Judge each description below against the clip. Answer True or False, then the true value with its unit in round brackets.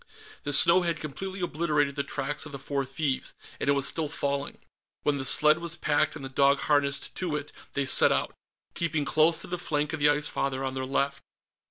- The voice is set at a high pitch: False (145 Hz)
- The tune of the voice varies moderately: False (2.2 semitones)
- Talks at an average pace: False (215 wpm)